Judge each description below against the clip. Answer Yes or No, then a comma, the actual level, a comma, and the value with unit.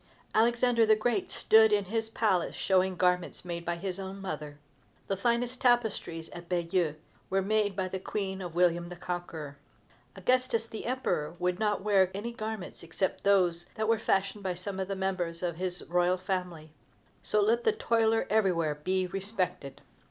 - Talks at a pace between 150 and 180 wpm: Yes, average, 165 wpm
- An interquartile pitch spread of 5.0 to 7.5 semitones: No, average, 3.5 semitones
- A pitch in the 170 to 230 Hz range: Yes, high, 190 Hz